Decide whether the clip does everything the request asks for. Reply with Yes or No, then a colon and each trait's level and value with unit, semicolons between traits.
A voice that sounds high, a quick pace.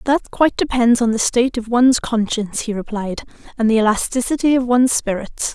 No: high, 240 Hz; average, 185 wpm